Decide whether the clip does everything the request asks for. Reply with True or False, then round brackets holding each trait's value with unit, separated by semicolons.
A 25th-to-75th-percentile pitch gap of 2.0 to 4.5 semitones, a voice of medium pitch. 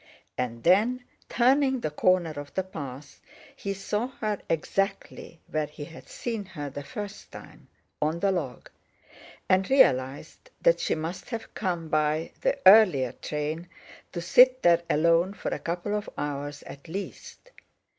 False (5.6 semitones; 175 Hz)